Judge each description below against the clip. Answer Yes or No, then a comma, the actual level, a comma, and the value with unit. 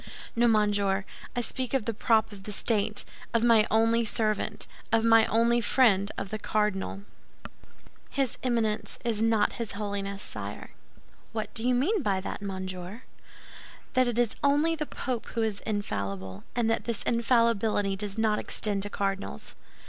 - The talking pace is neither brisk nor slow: Yes, average, 155 wpm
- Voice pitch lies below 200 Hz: No, high, 220 Hz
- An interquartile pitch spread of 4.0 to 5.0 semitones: No, narrow, 2.5 semitones